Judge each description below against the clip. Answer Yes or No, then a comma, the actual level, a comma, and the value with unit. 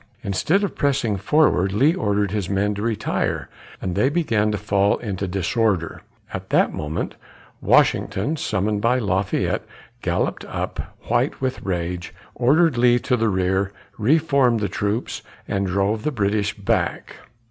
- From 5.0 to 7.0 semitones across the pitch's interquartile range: No, average, 4.2 semitones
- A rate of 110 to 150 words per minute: Yes, average, 145 wpm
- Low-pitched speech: Yes, low, 105 Hz